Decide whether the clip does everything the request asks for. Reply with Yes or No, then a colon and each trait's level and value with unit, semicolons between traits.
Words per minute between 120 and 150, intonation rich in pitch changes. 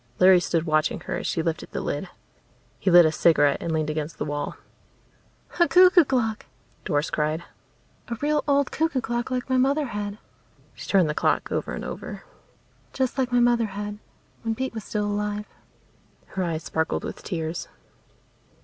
No: average, 175 wpm; wide, 7.5 semitones